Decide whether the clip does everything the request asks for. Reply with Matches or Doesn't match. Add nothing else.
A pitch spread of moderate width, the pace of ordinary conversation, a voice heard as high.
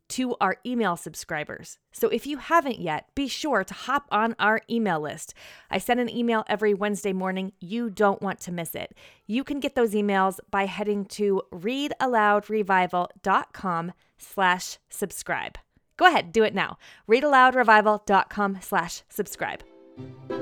Matches